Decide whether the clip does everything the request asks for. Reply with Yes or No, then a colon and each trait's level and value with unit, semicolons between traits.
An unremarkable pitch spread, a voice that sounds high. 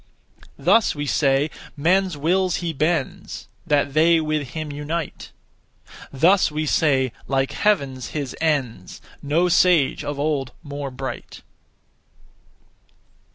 No: average, 3.3 semitones; medium, 150 Hz